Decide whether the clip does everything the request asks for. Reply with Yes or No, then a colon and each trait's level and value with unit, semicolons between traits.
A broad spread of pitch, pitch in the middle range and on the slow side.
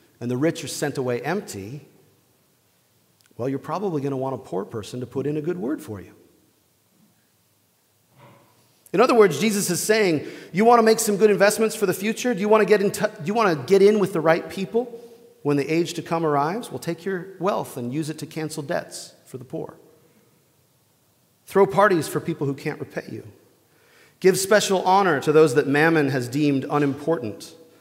No: wide, 5.9 semitones; medium, 165 Hz; fast, 205 wpm